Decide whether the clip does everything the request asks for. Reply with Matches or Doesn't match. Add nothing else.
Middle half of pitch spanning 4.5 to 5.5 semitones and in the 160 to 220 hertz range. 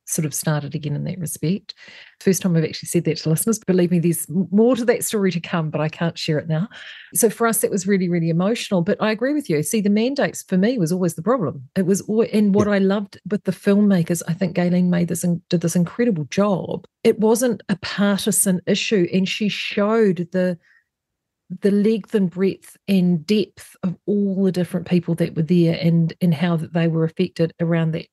Doesn't match